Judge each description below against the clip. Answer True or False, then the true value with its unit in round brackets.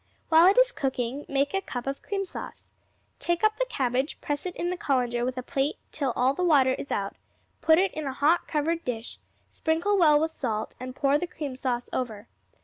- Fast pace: True (215 wpm)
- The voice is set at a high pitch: True (285 Hz)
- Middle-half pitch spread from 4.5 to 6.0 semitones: True (4.9 semitones)